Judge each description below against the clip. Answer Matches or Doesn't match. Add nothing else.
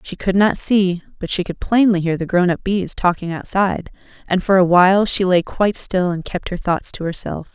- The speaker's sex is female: Matches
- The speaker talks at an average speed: Doesn't match